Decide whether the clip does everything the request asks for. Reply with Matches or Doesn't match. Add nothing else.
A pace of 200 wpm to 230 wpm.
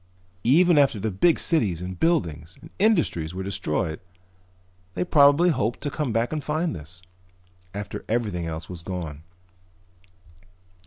Doesn't match